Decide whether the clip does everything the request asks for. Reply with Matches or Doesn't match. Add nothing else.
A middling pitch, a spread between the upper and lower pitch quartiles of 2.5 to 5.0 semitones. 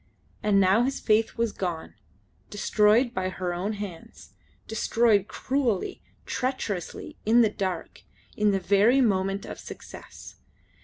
Doesn't match